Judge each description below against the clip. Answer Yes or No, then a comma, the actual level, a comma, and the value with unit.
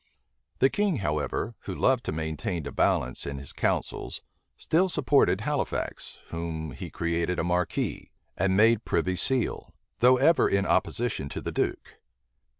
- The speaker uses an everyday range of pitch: No, wide, 7.8 semitones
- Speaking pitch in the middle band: No, very low, 95 Hz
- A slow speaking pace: No, average, 150 wpm